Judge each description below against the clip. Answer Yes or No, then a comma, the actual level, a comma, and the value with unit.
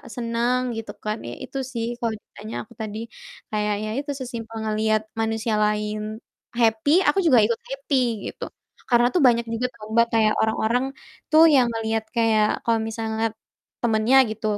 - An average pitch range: No, narrow, 1.7 semitones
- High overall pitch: Yes, high, 225 Hz